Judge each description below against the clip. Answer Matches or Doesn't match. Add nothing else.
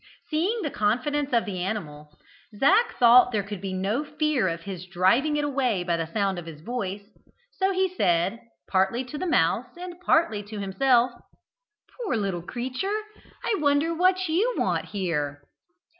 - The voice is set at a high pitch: Matches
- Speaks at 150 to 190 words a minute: Matches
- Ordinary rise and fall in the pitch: Doesn't match